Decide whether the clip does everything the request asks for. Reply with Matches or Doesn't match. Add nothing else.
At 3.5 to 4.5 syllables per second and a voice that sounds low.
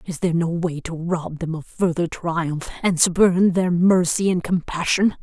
Doesn't match